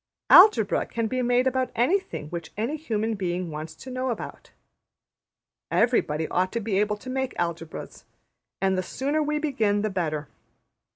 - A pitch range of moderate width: No, wide, 6.2 semitones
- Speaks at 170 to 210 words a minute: No, average, 160 wpm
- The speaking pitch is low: No, high, 220 Hz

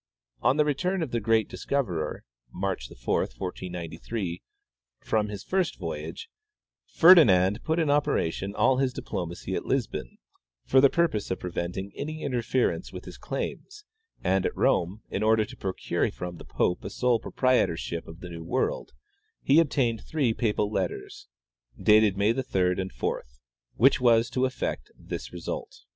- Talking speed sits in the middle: Yes, average, 155 wpm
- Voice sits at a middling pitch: No, low, 110 Hz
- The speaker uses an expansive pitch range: Yes, wide, 6.8 semitones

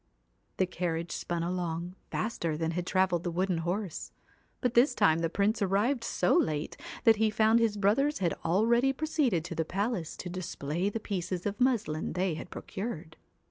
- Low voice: No, medium, 185 Hz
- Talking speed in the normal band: Yes, average, 175 wpm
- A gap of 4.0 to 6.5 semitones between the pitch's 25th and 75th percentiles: Yes, average, 4.6 semitones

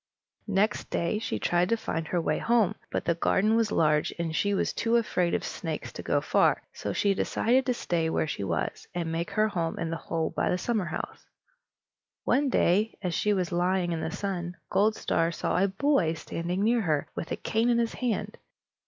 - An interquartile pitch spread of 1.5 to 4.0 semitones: No, average, 4.6 semitones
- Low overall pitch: No, medium, 185 Hz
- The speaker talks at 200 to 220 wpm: Yes, fast, 205 wpm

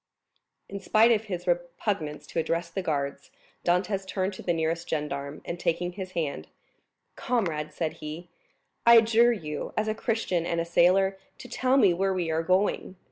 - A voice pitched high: No, medium, 175 Hz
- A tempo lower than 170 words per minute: No, average, 175 wpm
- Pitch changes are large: No, average, 3.5 semitones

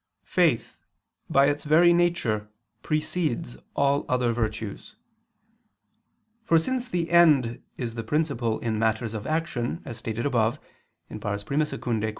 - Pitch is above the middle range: No, low, 130 Hz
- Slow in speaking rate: Yes, slow, 130 wpm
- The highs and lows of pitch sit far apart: Yes, wide, 6.0 semitones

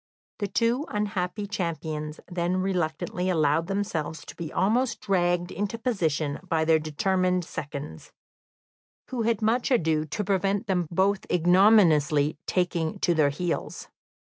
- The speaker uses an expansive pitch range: No, average, 4.2 semitones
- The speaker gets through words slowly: Yes, slow, 130 wpm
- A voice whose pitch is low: No, medium, 180 Hz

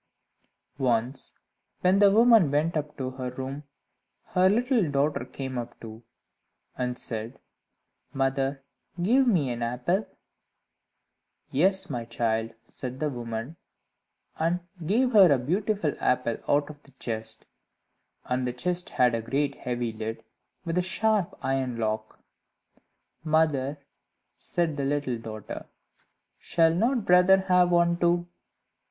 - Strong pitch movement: Yes, wide, 6.3 semitones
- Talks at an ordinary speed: No, slow, 130 wpm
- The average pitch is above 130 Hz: Yes, medium, 140 Hz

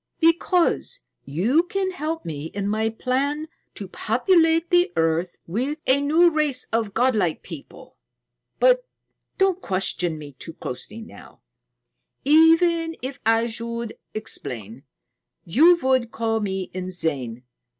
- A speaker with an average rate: No, slow, 120 wpm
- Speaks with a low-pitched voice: No, high, 235 Hz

